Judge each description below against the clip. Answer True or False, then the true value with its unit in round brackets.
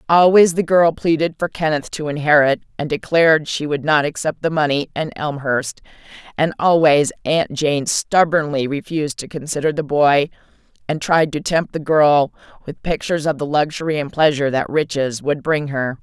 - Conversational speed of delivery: True (170 wpm)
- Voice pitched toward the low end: False (150 Hz)